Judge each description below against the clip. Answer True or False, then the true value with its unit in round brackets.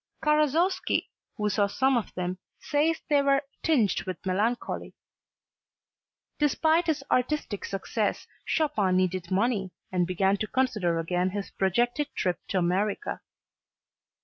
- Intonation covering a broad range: True (7.2 semitones)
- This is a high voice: True (210 Hz)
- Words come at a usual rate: False (120 wpm)